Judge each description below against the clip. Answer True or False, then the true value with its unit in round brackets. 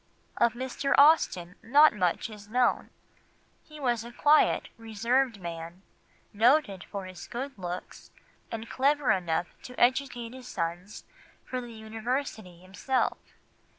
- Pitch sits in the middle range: False (230 Hz)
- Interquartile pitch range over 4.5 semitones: True (5.6 semitones)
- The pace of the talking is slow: True (125 wpm)